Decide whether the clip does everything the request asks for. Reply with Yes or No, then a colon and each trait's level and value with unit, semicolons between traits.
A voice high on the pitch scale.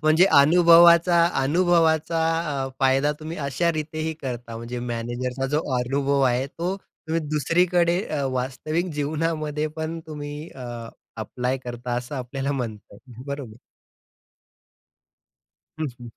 No: medium, 145 Hz